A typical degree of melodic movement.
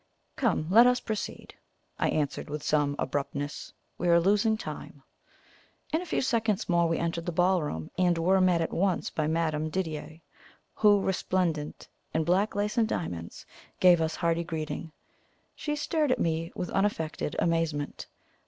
Yes: average, 4.1 semitones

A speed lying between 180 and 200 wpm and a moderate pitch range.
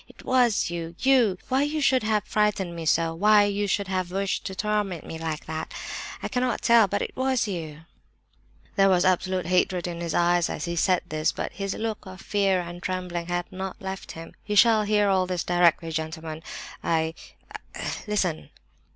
Yes: average, 185 wpm; average, 3.5 semitones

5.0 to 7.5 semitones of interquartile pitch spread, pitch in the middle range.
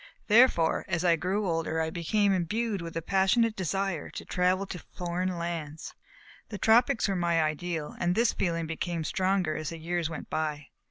No: average, 3.0 semitones; medium, 175 Hz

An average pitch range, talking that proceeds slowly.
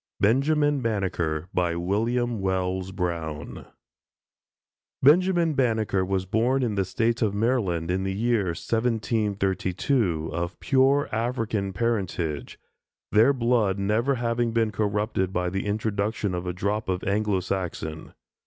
Yes: average, 4.1 semitones; slow, 120 wpm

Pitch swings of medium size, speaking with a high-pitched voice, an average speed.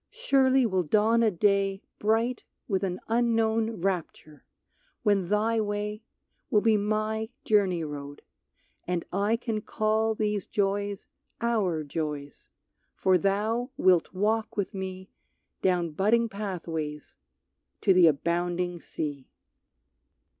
No: average, 3.7 semitones; high, 200 Hz; slow, 115 wpm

